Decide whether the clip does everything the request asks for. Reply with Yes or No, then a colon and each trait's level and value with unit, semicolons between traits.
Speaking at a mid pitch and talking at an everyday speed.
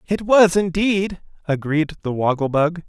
Yes: medium, 170 Hz; average, 145 wpm